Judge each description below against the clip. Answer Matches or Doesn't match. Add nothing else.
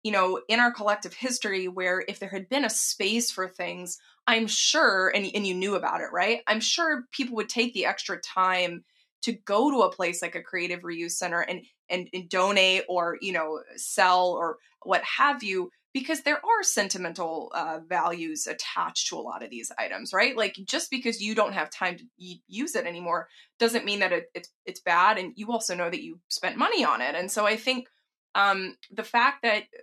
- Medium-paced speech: Doesn't match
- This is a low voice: Doesn't match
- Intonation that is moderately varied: Matches